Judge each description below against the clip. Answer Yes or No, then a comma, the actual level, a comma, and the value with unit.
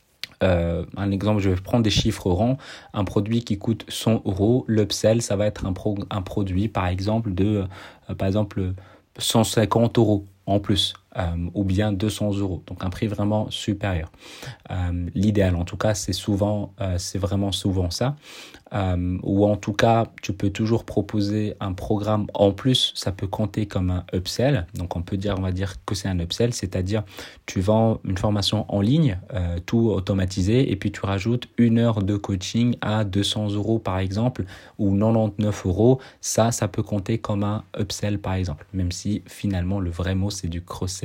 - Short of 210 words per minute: Yes, average, 190 wpm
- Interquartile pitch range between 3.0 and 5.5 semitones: No, narrow, 2.4 semitones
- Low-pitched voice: Yes, low, 100 Hz